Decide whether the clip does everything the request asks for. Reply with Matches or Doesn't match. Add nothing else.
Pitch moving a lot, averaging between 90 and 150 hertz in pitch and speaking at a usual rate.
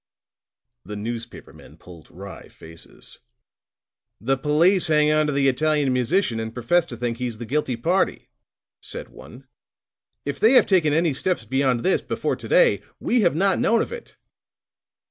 Matches